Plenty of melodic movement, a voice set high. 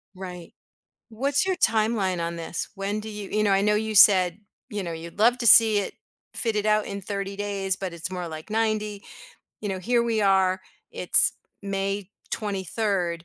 No: narrow, 2.5 semitones; high, 200 Hz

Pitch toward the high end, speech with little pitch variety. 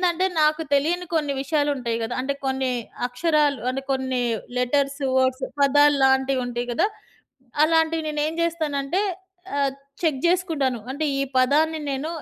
No: very high, 280 Hz; average, 3.2 semitones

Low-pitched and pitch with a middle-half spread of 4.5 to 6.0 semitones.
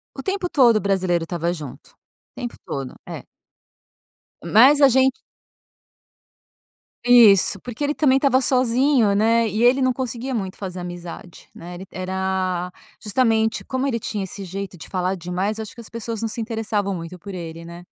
No: high, 210 Hz; average, 5.1 semitones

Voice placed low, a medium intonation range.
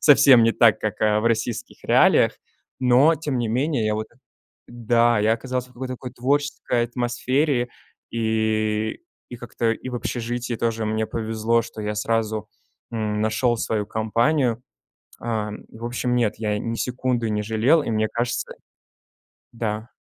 No: low, 115 Hz; narrow, 2.1 semitones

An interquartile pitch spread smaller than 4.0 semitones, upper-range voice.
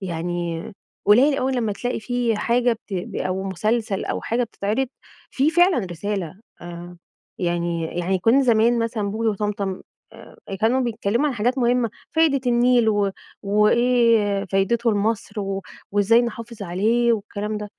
Yes: average, 3.6 semitones; high, 215 Hz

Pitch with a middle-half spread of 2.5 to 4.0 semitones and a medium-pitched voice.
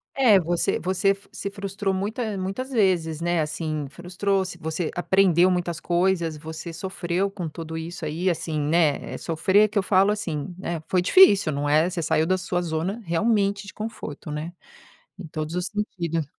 Yes: average, 3.4 semitones; medium, 175 Hz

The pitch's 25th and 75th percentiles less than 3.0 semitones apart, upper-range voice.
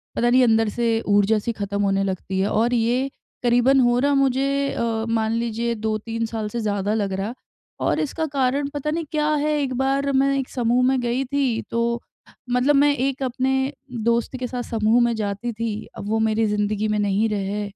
No: average, 3.6 semitones; high, 235 Hz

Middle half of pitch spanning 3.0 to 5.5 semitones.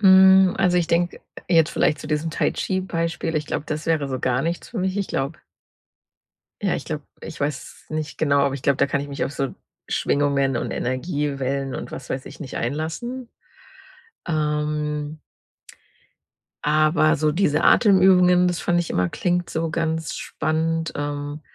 Yes: average, 3.3 semitones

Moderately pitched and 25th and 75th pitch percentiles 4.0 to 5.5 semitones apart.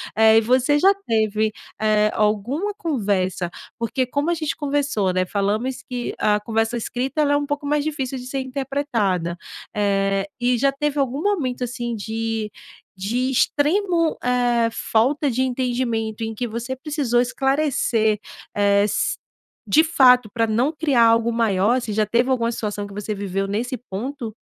No: high, 240 Hz; average, 4.3 semitones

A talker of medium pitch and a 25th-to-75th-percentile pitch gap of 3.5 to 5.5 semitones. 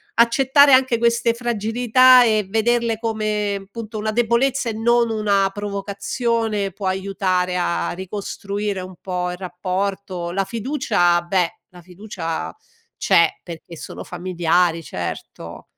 No: high, 205 Hz; average, 4.1 semitones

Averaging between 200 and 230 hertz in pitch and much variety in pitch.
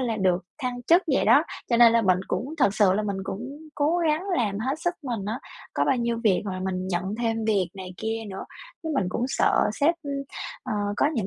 No: high, 225 Hz; average, 4.8 semitones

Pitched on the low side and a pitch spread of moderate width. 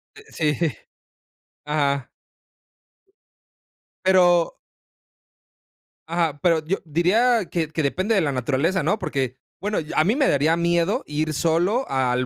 No: medium, 165 Hz; average, 4.1 semitones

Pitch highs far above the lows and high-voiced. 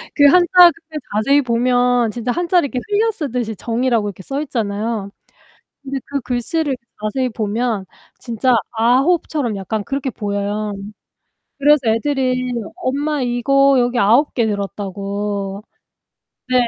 No: average, 4.6 semitones; high, 245 Hz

